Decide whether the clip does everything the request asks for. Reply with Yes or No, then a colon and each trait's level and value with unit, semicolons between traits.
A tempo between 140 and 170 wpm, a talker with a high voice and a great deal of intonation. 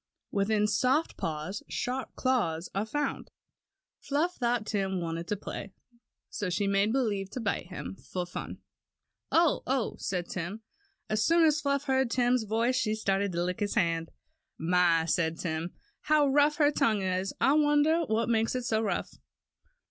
Yes: average, 165 wpm; high, 215 Hz; wide, 6.2 semitones